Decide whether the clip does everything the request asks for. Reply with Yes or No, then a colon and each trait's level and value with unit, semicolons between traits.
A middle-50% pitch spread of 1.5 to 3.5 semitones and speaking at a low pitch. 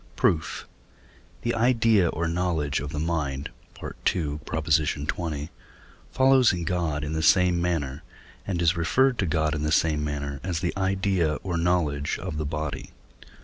Yes: average, 3.2 semitones; very low, 80 Hz